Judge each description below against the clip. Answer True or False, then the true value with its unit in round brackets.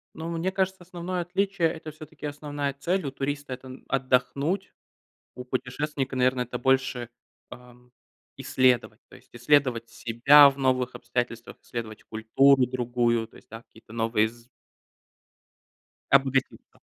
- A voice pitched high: False (130 Hz)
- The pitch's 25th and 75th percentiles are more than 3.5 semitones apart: False (3.2 semitones)